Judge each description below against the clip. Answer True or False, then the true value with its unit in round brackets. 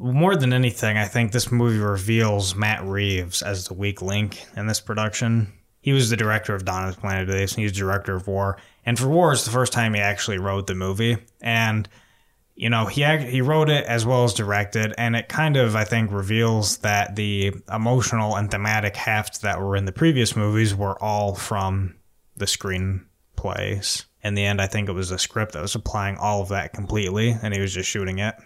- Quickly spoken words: True (215 wpm)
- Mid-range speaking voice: False (105 Hz)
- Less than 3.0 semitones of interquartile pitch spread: True (2.6 semitones)